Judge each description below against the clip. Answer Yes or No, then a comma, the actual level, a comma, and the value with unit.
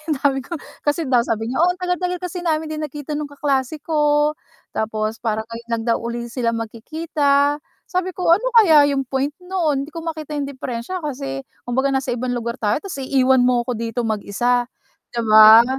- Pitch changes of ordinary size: Yes, average, 4.5 semitones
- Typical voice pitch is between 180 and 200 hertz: No, very high, 270 Hz